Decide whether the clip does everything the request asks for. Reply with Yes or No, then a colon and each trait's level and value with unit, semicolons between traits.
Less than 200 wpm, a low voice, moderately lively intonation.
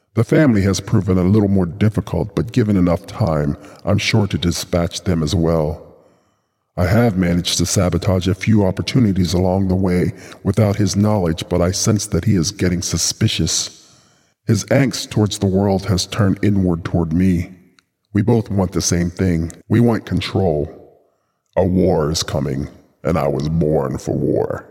Yes: average, 170 wpm; very low, 95 Hz; average, 3.2 semitones